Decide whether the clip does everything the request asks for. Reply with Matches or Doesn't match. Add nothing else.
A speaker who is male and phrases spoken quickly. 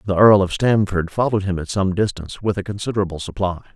Matches